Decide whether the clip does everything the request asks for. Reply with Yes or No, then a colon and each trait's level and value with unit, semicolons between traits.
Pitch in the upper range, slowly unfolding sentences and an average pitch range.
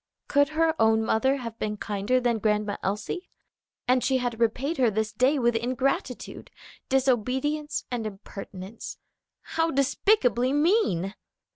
Yes: very high, 250 Hz; slow, 130 wpm; average, 4.0 semitones